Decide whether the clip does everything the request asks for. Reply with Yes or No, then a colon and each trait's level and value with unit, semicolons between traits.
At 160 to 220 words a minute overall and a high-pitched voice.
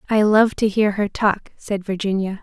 Yes: average, 200 wpm; high, 205 Hz